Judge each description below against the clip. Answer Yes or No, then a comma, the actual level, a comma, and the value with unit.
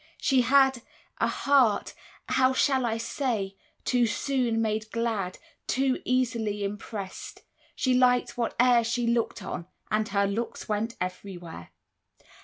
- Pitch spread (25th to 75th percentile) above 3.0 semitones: Yes, average, 3.4 semitones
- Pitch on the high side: Yes, high, 230 Hz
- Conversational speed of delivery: No, slow, 125 wpm